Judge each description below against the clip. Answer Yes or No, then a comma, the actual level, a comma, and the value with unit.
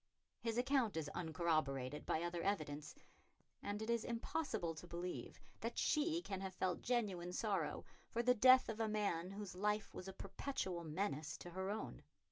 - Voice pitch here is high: Yes, high, 195 Hz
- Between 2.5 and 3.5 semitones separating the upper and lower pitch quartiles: No, average, 4.8 semitones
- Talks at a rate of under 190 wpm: Yes, average, 170 wpm